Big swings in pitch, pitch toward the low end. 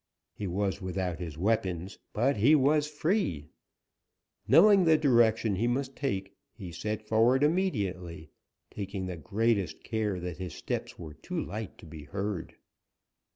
Yes: wide, 6.1 semitones; low, 105 Hz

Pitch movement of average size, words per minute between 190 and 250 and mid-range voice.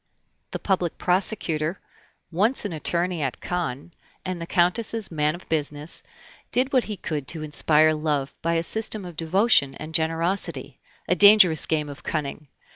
No: average, 3.5 semitones; average, 155 wpm; medium, 165 Hz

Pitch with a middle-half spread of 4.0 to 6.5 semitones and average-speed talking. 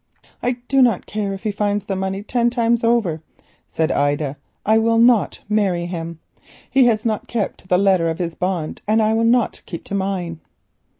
Yes: average, 4.4 semitones; average, 195 wpm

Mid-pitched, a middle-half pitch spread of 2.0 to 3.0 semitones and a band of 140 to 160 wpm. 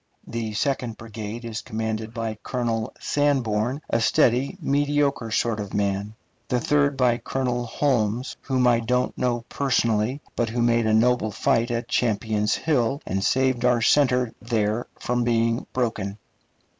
No: low, 120 Hz; narrow, 2.4 semitones; average, 145 wpm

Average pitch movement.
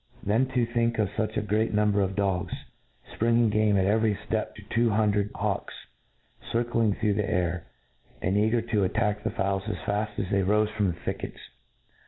No: narrow, 1.8 semitones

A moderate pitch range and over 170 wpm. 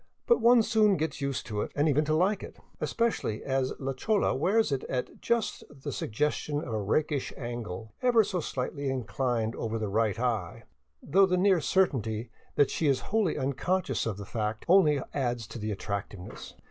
No: wide, 8.1 semitones; average, 185 wpm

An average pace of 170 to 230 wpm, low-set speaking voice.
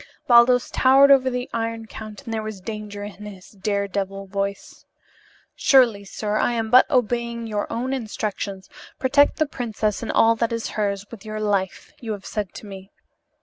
No: average, 180 wpm; high, 220 Hz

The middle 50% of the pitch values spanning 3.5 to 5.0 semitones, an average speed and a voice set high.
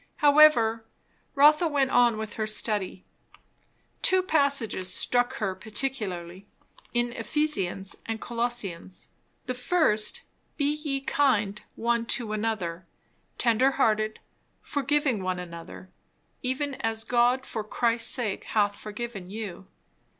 No: average, 4.5 semitones; slow, 115 wpm; high, 230 Hz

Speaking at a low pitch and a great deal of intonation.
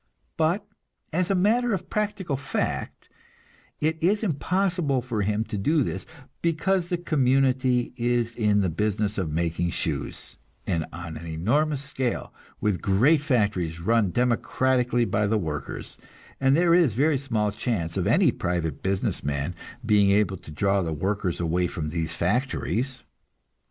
Yes: low, 115 Hz; wide, 8.1 semitones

